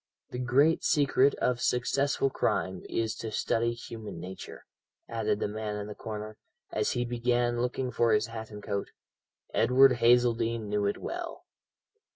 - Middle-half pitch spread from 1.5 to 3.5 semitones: Yes, narrow, 2.6 semitones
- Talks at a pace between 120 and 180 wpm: Yes, average, 155 wpm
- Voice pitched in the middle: No, low, 115 Hz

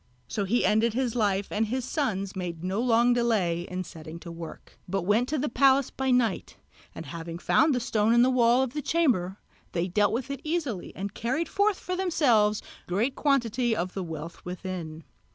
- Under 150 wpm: No, average, 195 wpm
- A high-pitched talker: Yes, high, 220 Hz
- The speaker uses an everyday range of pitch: No, wide, 5.9 semitones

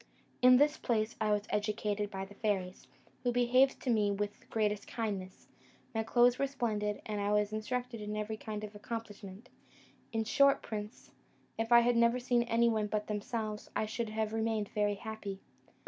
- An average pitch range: No, narrow, 2.2 semitones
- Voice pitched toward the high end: Yes, high, 215 Hz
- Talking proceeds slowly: No, average, 180 wpm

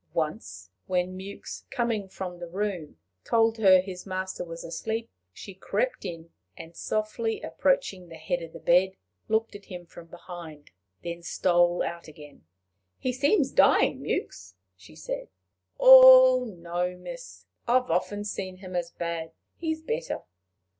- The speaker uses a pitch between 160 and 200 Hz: Yes, medium, 185 Hz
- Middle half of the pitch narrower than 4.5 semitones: No, average, 4.9 semitones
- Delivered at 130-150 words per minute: Yes, average, 145 wpm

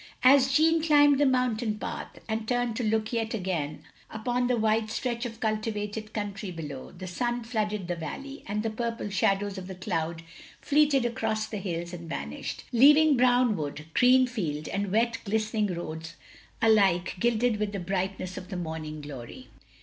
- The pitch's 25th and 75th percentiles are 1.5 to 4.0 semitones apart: No, average, 4.8 semitones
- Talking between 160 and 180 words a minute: Yes, average, 170 wpm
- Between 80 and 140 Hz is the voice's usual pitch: No, high, 215 Hz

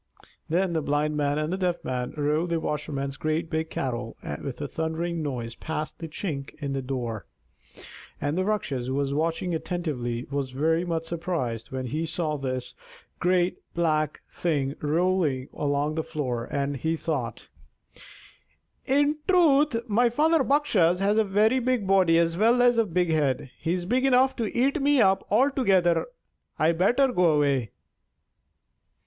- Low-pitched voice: No, medium, 165 Hz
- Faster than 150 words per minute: Yes, average, 160 wpm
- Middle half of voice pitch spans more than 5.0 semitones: Yes, wide, 5.4 semitones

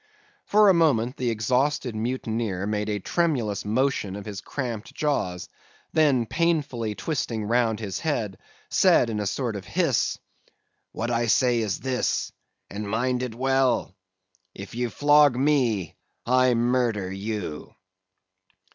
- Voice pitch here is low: Yes, low, 115 Hz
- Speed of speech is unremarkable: No, slow, 130 wpm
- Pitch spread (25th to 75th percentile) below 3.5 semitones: No, average, 3.9 semitones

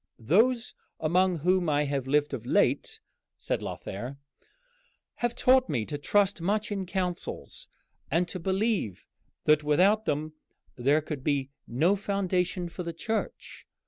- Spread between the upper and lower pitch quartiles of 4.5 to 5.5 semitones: Yes, average, 5.2 semitones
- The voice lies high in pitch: No, medium, 175 Hz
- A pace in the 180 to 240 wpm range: No, average, 140 wpm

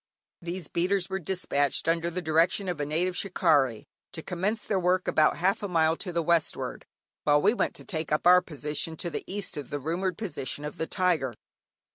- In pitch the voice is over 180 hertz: No, medium, 170 Hz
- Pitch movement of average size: Yes, average, 3.2 semitones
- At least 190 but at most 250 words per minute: Yes, average, 200 wpm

